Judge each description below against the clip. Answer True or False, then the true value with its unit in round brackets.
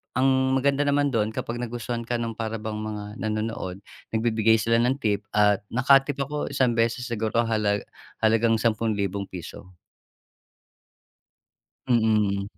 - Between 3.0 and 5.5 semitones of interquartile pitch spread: False (2.4 semitones)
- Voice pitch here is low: True (115 Hz)